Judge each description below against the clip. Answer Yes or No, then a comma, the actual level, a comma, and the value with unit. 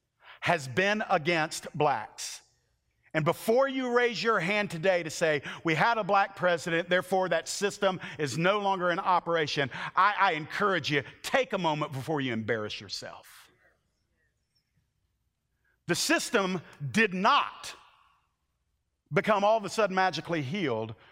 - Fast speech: No, slow, 135 wpm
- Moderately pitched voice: Yes, medium, 180 Hz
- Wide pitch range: No, average, 4.5 semitones